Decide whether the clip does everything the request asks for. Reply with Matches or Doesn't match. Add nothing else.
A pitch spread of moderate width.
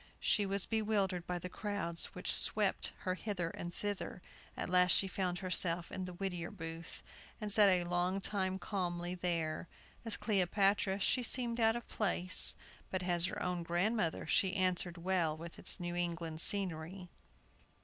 Doesn't match